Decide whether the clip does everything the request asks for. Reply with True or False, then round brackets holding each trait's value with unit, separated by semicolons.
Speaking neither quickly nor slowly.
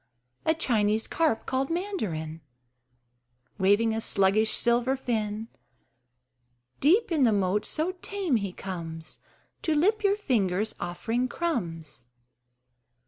False (110 wpm)